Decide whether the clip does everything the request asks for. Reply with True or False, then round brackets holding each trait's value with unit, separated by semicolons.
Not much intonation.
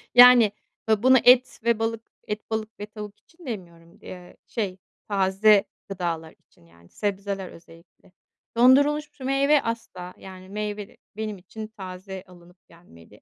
False (3.8 semitones)